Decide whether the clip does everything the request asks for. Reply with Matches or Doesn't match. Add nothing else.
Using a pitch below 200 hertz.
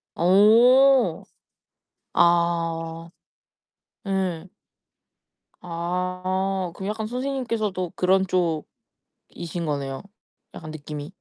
Matches